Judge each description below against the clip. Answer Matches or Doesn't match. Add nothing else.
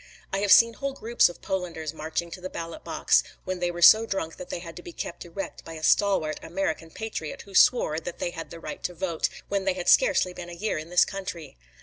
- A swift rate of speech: Matches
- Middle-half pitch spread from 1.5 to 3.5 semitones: Matches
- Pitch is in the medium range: Matches